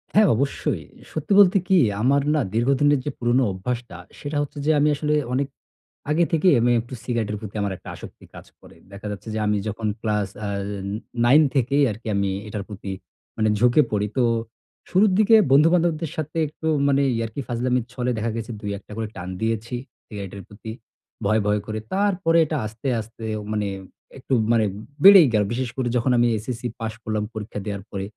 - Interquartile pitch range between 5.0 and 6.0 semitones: Yes, average, 5.3 semitones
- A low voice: Yes, low, 120 Hz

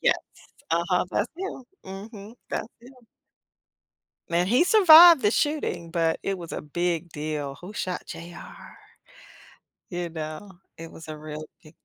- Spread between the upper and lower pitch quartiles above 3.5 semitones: Yes, average, 5.1 semitones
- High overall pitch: No, medium, 175 Hz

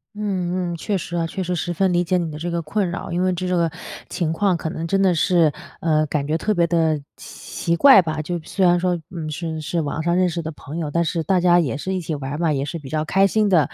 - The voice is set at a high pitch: No, medium, 170 Hz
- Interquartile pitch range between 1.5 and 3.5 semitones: Yes, narrow, 2.4 semitones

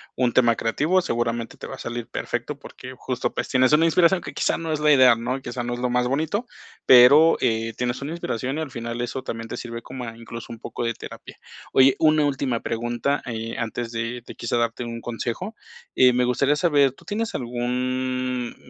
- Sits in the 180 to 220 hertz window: No, low, 125 Hz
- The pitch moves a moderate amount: Yes, average, 3.0 semitones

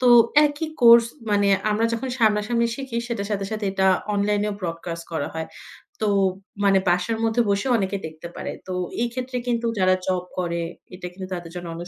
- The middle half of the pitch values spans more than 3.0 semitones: Yes, average, 4.5 semitones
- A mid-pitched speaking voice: No, high, 200 Hz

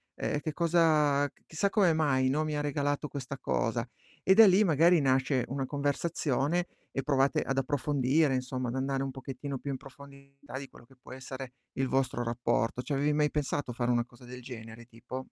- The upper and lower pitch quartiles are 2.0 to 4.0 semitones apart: Yes, narrow, 2.5 semitones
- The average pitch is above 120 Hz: Yes, low, 135 Hz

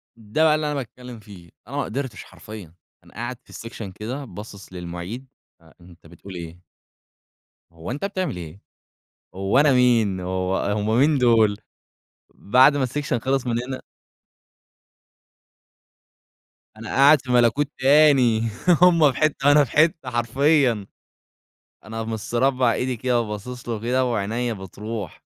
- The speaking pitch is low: Yes, low, 120 Hz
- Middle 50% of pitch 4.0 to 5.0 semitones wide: Yes, average, 4.7 semitones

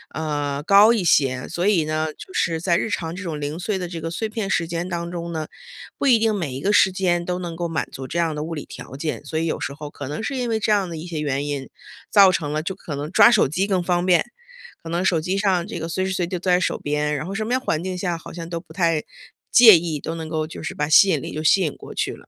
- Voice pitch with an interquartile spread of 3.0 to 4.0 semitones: Yes, average, 3.3 semitones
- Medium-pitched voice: Yes, medium, 170 Hz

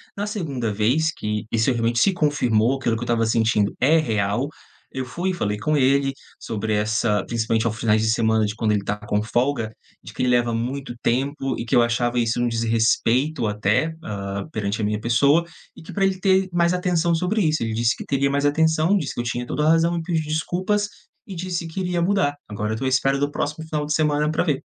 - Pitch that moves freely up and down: Yes, wide, 6.1 semitones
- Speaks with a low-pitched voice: Yes, low, 130 Hz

